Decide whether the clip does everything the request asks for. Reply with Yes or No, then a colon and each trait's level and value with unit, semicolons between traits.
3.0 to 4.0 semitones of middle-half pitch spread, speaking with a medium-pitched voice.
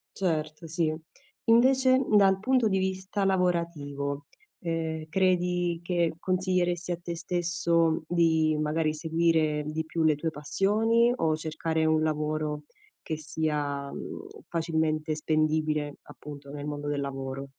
No: narrow, 2.5 semitones; medium, 160 Hz